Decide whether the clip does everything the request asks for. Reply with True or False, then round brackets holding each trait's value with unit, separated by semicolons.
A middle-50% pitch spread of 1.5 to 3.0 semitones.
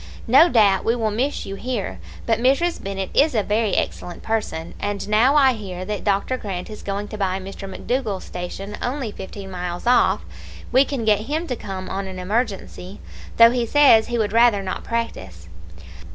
False (4.0 semitones)